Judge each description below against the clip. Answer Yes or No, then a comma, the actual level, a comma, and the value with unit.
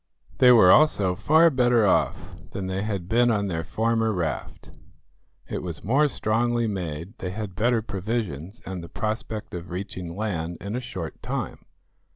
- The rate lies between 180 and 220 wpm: No, average, 165 wpm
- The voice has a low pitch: Yes, low, 105 Hz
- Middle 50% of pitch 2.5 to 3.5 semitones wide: No, average, 4.4 semitones